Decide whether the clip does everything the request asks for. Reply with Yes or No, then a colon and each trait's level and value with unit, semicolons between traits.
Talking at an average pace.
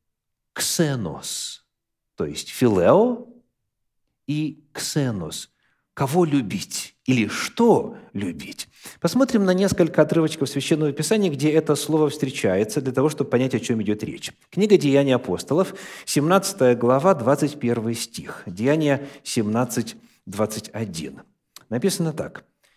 No: slow, 105 wpm